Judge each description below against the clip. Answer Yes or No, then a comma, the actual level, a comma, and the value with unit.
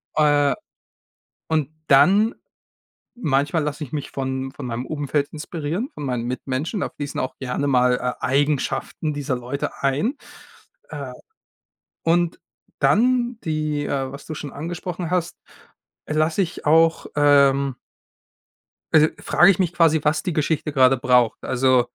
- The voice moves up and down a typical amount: Yes, average, 3.3 semitones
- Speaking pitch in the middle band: Yes, medium, 145 Hz